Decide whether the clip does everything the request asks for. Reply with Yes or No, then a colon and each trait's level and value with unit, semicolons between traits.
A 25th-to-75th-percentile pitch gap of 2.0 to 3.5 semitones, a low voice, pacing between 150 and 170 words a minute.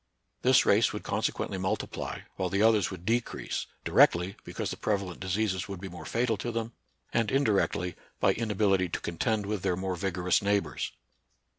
Yes: average, 2.9 semitones; low, 100 Hz; average, 165 wpm